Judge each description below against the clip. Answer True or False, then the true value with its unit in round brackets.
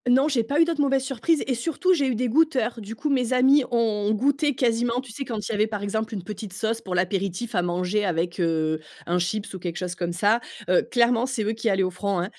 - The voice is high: True (220 Hz)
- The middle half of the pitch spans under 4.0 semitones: False (5.4 semitones)